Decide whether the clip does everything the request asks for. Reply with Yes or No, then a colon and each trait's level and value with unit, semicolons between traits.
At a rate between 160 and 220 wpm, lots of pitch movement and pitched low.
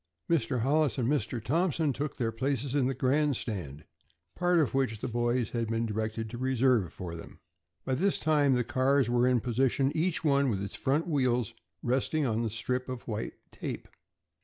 No: average, 185 wpm; average, 3.6 semitones; low, 130 Hz